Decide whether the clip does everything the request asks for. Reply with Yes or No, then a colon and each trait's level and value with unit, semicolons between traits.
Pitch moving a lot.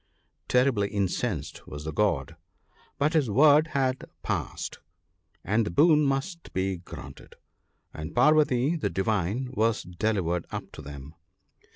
Yes: wide, 7.7 semitones